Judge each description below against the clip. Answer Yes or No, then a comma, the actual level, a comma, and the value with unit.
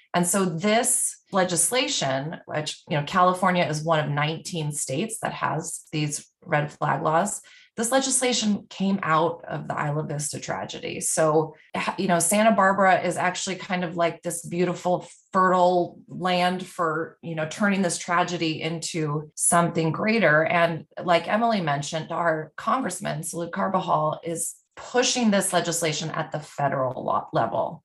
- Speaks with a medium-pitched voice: Yes, medium, 170 Hz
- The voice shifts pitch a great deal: No, average, 2.9 semitones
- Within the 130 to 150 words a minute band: Yes, average, 145 wpm